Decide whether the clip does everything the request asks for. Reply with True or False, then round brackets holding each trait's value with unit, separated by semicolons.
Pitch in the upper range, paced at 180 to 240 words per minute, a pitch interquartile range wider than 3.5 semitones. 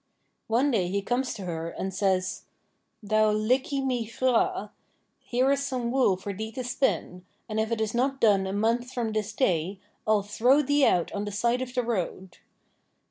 True (220 Hz; 190 wpm; 4.0 semitones)